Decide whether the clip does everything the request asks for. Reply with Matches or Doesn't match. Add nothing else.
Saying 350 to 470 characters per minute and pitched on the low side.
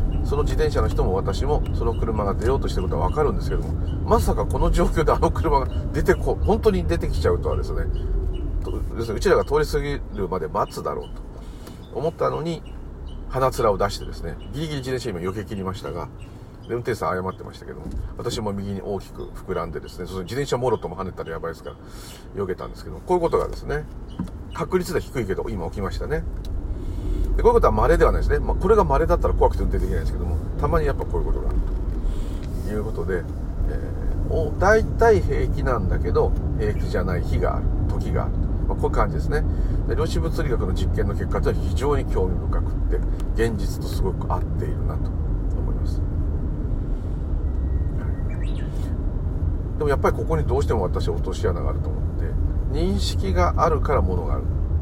Matches